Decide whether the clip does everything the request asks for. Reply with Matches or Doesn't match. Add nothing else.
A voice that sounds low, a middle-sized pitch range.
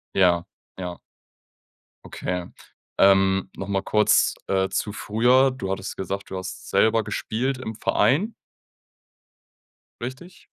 Matches